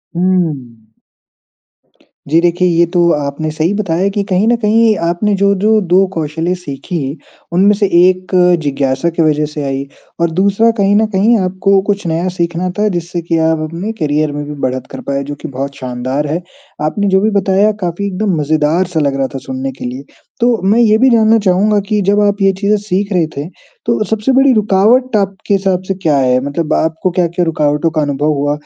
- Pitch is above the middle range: No, medium, 175 Hz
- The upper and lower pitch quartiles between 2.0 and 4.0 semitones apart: No, average, 5.1 semitones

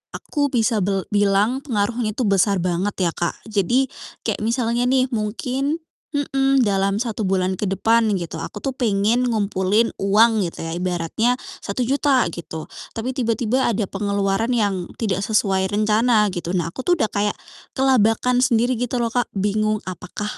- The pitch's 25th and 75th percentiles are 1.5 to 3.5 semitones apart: No, average, 4.0 semitones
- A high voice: Yes, high, 215 Hz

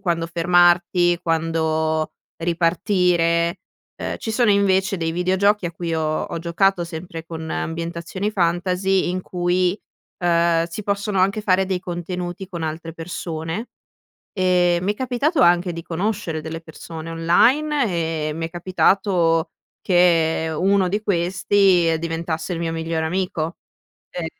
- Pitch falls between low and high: Yes, medium, 175 Hz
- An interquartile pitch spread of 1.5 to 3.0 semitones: Yes, narrow, 2.4 semitones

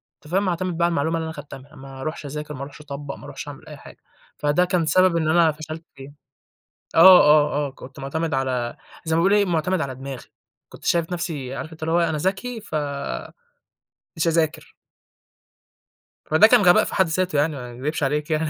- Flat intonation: No, average, 3.2 semitones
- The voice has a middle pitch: Yes, medium, 155 Hz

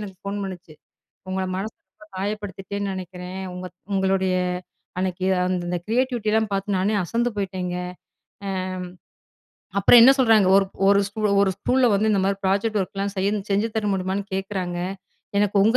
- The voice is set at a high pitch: Yes, high, 195 Hz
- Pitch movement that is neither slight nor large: No, narrow, 2.1 semitones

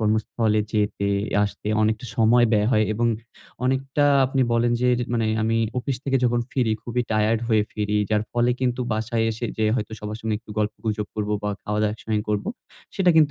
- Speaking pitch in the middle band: No, low, 110 Hz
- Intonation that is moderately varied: No, narrow, 2.2 semitones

